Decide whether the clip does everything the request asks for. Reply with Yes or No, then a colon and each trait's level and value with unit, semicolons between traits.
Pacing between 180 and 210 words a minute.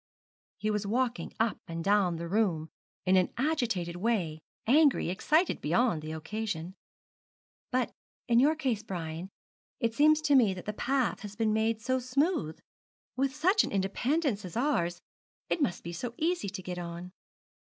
No: average, 160 wpm